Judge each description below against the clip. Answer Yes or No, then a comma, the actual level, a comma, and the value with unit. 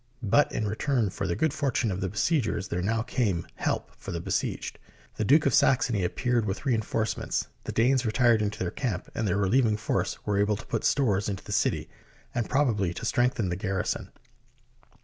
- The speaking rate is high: Yes, fast, 210 wpm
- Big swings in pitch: No, average, 4.1 semitones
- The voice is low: Yes, low, 110 Hz